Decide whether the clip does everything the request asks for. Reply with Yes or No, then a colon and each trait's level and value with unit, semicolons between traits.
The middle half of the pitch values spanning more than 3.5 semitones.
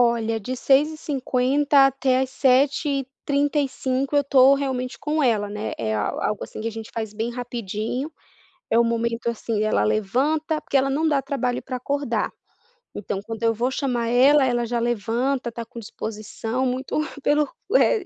No: average, 3.2 semitones